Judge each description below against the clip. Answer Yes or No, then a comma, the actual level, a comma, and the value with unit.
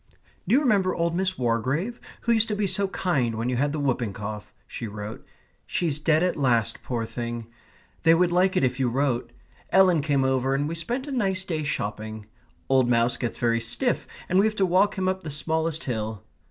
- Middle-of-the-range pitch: Yes, medium, 145 Hz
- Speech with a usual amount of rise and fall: No, wide, 7.7 semitones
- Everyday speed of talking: No, fast, 210 wpm